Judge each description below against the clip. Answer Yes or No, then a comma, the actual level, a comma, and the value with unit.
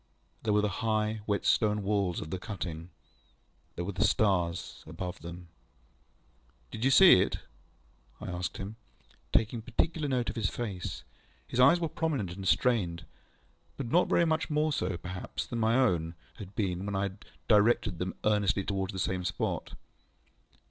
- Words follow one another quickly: No, average, 165 wpm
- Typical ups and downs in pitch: Yes, average, 4.2 semitones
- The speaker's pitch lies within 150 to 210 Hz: No, low, 100 Hz